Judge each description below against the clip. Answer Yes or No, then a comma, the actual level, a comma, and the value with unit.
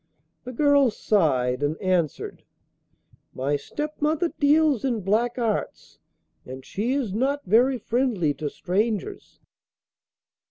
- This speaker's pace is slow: Yes, slow, 110 wpm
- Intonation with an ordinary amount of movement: No, wide, 7.9 semitones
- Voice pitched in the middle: No, high, 225 Hz